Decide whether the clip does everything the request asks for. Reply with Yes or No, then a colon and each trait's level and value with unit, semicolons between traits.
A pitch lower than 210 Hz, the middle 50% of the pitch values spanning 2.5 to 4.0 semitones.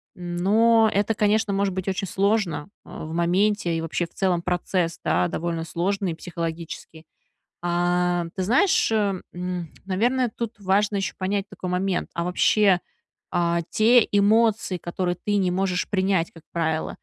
Yes: medium, 185 Hz; average, 2.9 semitones